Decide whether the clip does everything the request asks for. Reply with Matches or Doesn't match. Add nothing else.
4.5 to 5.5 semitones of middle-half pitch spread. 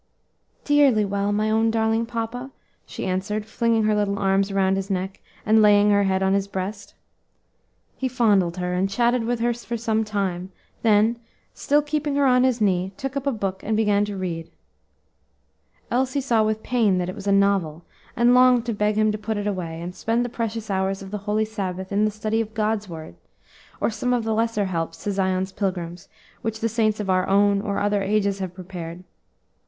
Doesn't match